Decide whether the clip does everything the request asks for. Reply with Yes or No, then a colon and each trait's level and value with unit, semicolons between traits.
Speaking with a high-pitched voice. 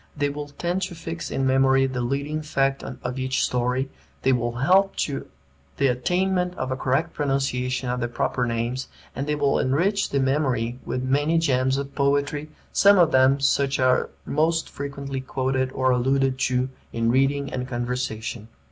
No: low, 135 Hz